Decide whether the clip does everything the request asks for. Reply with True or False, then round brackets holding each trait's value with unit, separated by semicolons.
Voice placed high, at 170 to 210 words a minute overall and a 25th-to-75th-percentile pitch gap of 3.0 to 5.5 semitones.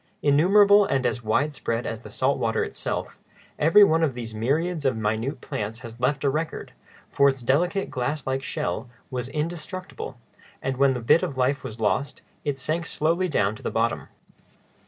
False (135 Hz; 180 wpm; 4.7 semitones)